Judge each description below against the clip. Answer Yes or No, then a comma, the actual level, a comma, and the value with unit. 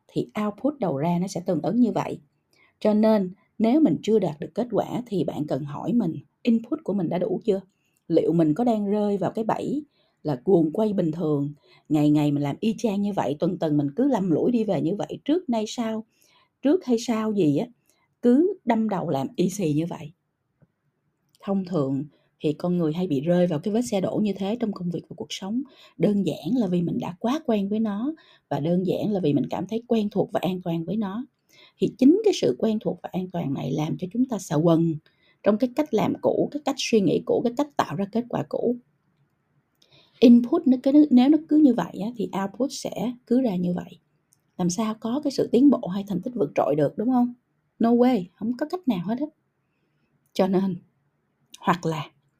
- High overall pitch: Yes, high, 200 Hz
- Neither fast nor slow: Yes, average, 225 wpm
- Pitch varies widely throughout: Yes, wide, 6.2 semitones